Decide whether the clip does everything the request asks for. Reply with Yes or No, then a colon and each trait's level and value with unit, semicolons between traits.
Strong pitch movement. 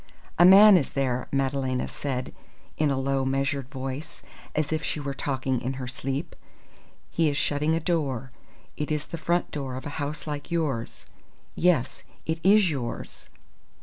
No: average, 3.0 semitones